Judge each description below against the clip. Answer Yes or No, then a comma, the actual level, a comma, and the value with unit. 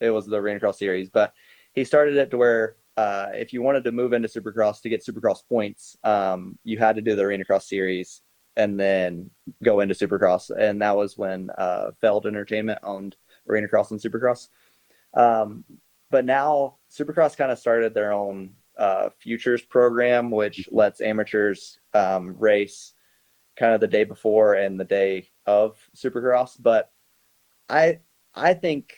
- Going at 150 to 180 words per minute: Yes, average, 170 wpm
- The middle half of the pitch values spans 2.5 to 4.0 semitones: Yes, average, 3.5 semitones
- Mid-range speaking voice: No, low, 110 Hz